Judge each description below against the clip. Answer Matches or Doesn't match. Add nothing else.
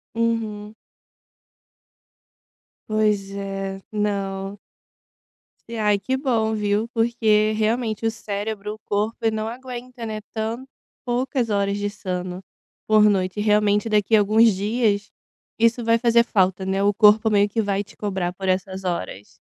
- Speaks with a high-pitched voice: Matches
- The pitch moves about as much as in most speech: Doesn't match